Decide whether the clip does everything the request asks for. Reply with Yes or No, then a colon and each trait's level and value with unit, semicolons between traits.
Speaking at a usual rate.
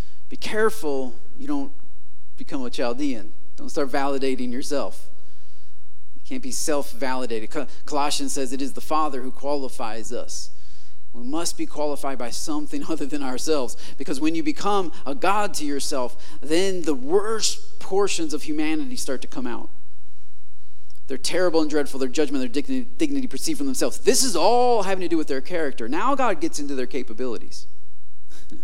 Yes: average, 165 wpm